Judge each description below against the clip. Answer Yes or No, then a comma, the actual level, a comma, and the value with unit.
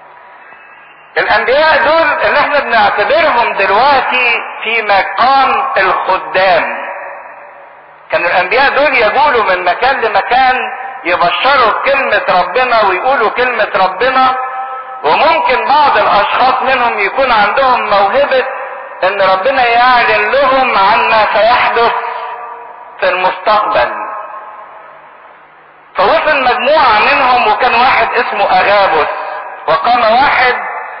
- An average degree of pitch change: Yes, average, 4.6 semitones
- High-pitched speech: Yes, high, 240 Hz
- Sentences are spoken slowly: Yes, slow, 90 wpm